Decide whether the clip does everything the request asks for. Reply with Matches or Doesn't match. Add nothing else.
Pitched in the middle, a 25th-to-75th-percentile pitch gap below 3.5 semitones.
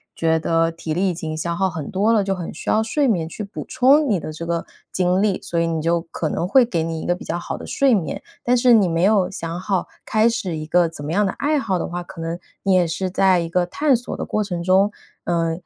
Doesn't match